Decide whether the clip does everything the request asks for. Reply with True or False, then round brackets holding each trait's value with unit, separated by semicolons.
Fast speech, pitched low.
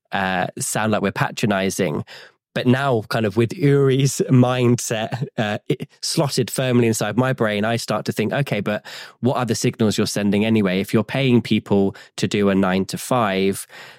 False (180 wpm; 115 Hz)